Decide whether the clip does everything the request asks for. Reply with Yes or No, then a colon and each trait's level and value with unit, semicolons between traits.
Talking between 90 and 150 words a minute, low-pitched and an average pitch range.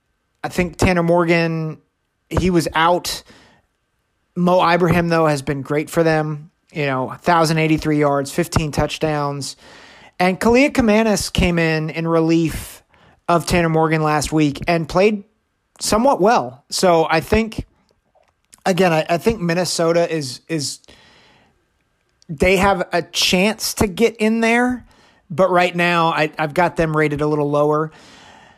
No: average, 140 wpm; medium, 165 Hz; average, 3.0 semitones